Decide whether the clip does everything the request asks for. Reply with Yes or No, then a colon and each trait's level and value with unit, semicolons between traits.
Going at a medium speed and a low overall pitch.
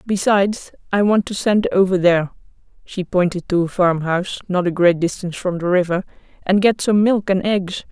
No: average, 190 wpm; medium, 185 Hz